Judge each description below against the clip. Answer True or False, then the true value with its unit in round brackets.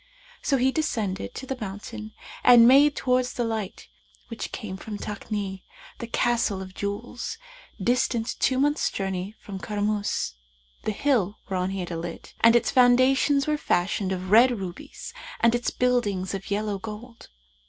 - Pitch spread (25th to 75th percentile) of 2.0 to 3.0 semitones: False (4.3 semitones)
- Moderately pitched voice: False (220 Hz)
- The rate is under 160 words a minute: True (150 wpm)